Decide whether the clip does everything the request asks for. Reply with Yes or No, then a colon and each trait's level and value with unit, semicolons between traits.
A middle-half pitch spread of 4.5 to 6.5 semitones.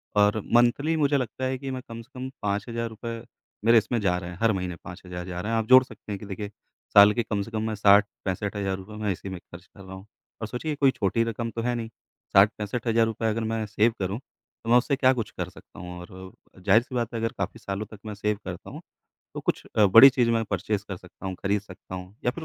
No: average, 3.1 semitones